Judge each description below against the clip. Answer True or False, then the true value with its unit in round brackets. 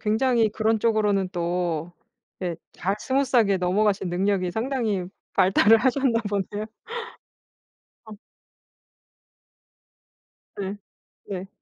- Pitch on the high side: True (205 Hz)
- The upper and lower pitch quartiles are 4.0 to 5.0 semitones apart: False (3.3 semitones)